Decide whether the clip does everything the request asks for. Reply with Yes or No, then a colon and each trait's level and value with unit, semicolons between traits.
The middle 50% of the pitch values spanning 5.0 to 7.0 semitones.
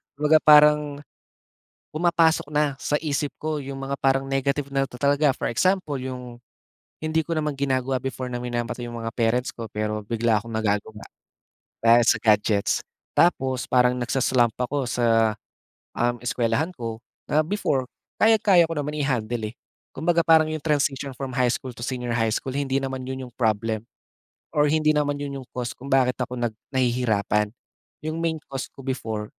No: average, 3.8 semitones